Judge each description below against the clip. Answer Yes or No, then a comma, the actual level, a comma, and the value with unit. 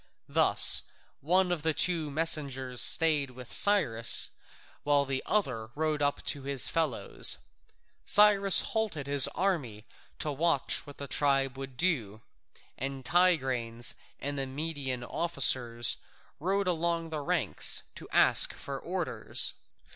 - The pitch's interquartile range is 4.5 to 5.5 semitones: No, average, 4.1 semitones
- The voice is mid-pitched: Yes, medium, 145 Hz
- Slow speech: Yes, slow, 125 wpm